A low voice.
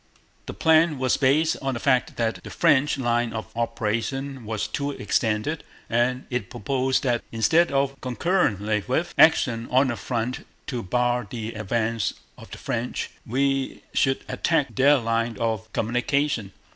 Yes: low, 125 Hz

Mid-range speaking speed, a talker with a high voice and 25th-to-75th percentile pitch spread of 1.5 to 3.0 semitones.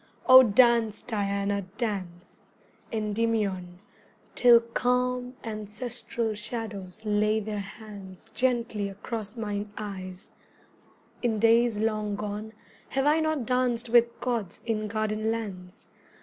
No: slow, 105 wpm; high, 215 Hz; narrow, 2.6 semitones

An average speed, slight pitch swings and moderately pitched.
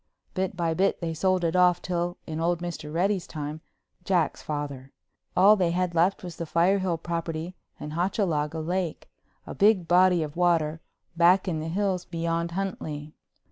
Yes: average, 155 wpm; narrow, 2.3 semitones; medium, 170 Hz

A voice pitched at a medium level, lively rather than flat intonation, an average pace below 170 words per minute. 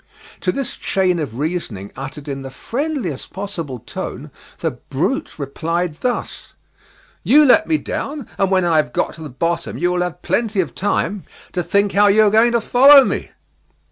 No: medium, 180 Hz; wide, 6.1 semitones; average, 180 wpm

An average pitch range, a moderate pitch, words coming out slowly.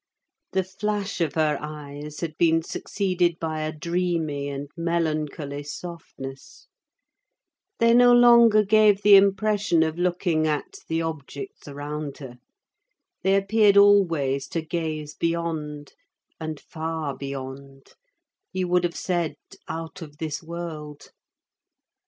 Yes: average, 3.9 semitones; medium, 165 Hz; slow, 115 wpm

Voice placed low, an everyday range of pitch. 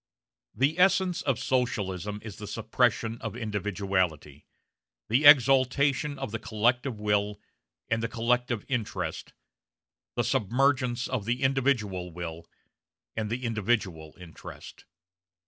Yes: low, 115 Hz; average, 4.0 semitones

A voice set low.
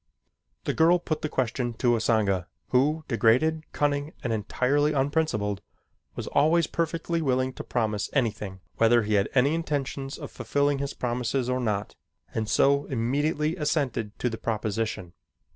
Yes: low, 130 Hz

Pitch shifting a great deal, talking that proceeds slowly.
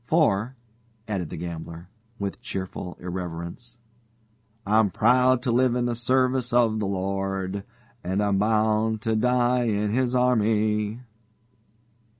No: average, 3.9 semitones; slow, 125 wpm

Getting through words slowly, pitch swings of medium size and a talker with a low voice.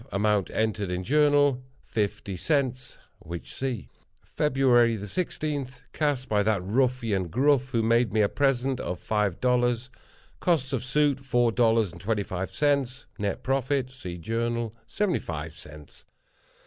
Yes: slow, 120 wpm; average, 4.5 semitones; low, 120 Hz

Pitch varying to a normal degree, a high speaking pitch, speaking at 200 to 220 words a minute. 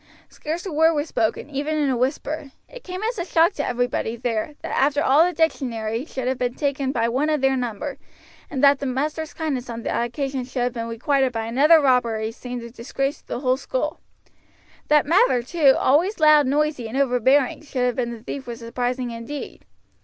Yes: average, 3.7 semitones; very high, 270 Hz; fast, 205 wpm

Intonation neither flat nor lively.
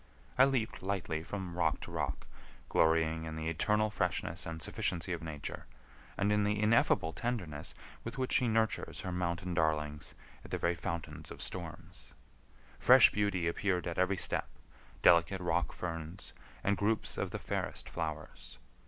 Yes: average, 4.0 semitones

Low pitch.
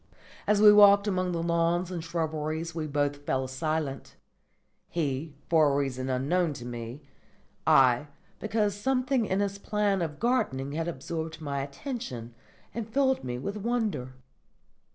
No: medium, 165 Hz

